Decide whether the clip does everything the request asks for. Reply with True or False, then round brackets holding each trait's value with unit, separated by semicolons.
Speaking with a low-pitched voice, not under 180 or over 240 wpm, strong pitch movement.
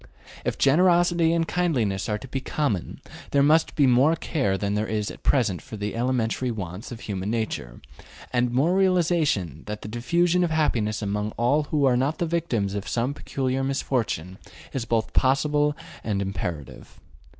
False (125 Hz; 170 wpm; 6.3 semitones)